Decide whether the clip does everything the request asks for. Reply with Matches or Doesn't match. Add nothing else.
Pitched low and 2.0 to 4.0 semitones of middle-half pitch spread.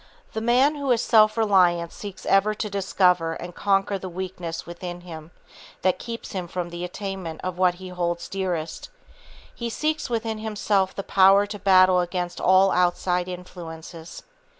Doesn't match